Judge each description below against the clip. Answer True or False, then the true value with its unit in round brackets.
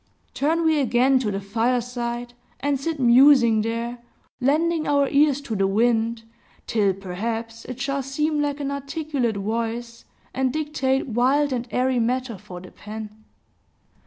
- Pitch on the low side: False (250 Hz)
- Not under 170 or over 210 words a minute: False (145 wpm)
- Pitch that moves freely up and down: False (3.6 semitones)